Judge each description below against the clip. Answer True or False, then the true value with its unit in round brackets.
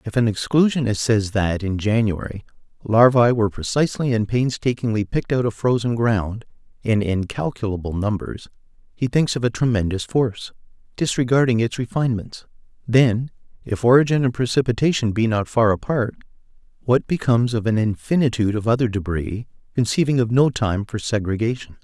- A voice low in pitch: True (115 Hz)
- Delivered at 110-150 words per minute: True (140 wpm)